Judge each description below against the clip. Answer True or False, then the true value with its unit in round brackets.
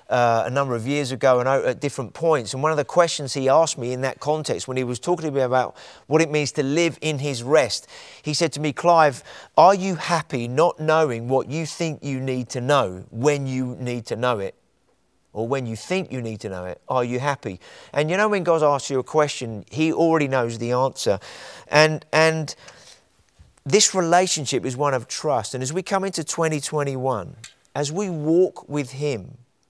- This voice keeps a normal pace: False (210 wpm)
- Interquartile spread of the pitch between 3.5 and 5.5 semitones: True (3.8 semitones)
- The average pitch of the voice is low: False (145 Hz)